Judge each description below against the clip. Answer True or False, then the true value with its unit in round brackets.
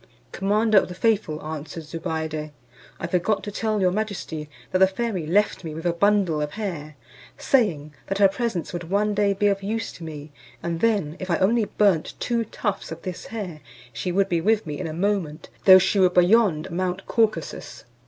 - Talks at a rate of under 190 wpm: False (195 wpm)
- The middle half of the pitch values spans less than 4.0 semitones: False (4.3 semitones)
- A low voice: False (185 Hz)